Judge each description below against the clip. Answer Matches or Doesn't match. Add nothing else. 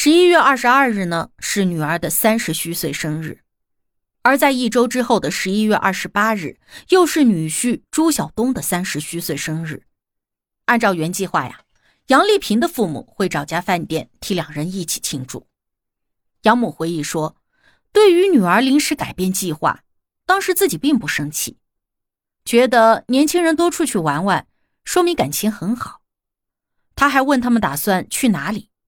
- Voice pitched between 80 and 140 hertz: Doesn't match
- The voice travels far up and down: Matches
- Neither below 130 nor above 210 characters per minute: Doesn't match